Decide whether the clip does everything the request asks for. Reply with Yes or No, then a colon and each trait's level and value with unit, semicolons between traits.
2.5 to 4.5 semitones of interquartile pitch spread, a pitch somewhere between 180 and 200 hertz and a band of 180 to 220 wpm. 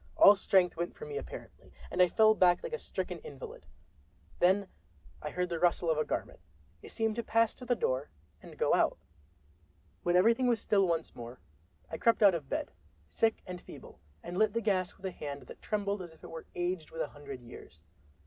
No: average, 5.0 semitones; medium, 185 Hz; fast, 205 wpm